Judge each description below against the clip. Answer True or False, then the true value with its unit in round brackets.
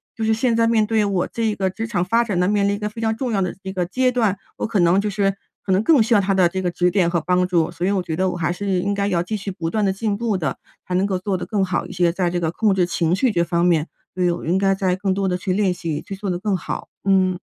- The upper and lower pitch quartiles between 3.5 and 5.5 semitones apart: False (2.7 semitones)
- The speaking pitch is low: False (190 Hz)